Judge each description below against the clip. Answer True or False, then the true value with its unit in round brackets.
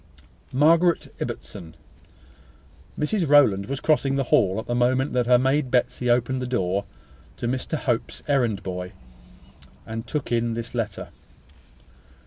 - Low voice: True (125 Hz)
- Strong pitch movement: False (3.3 semitones)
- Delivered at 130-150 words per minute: True (135 wpm)